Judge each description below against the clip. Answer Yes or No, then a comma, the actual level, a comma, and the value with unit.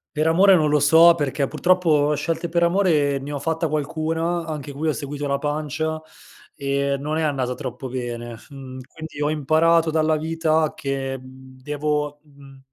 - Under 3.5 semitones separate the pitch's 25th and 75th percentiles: Yes, narrow, 2.6 semitones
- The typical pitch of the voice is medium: Yes, medium, 150 Hz